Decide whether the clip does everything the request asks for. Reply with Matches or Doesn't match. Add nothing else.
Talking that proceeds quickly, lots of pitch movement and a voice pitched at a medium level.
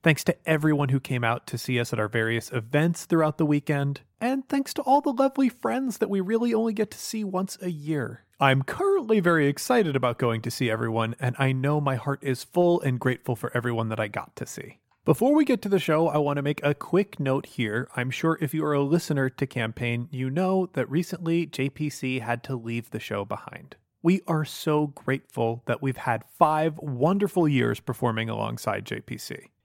Matches